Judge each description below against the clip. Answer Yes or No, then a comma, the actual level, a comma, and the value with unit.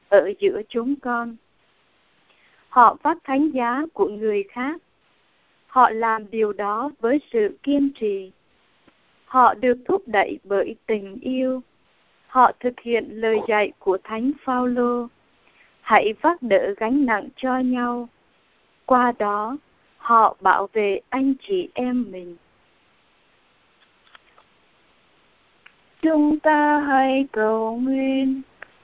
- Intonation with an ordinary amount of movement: Yes, average, 4.2 semitones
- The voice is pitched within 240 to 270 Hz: Yes, very high, 250 Hz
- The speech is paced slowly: Yes, slow, 115 wpm